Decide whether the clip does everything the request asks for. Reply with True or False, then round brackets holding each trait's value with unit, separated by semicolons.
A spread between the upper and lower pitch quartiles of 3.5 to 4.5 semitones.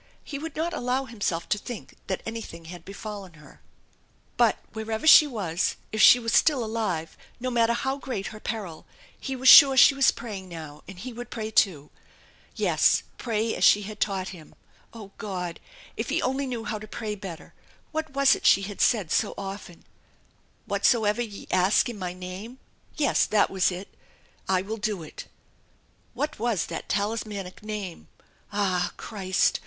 True (4.2 semitones)